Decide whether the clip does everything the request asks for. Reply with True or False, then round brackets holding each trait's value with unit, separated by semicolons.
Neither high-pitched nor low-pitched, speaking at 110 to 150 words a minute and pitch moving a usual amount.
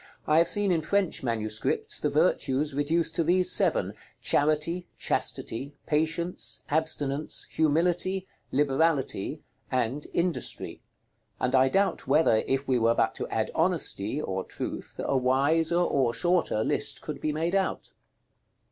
True (150 Hz; 135 wpm; 4.2 semitones)